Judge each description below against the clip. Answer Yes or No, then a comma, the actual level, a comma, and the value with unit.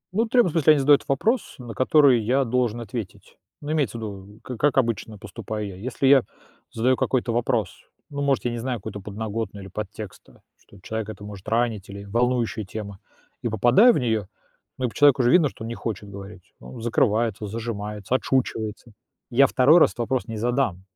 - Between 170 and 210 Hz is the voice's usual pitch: No, low, 115 Hz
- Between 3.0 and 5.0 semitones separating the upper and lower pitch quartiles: Yes, average, 3.7 semitones